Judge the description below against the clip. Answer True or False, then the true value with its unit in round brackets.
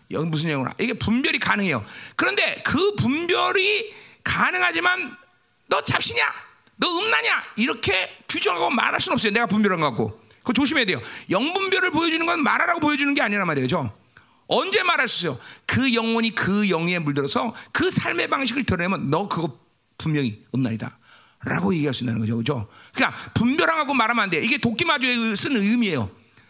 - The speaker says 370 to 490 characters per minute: True (375 characters per minute)